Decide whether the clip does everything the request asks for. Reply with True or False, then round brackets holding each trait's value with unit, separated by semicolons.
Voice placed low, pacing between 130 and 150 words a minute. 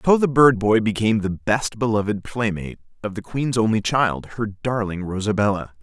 False (110 Hz; 175 wpm)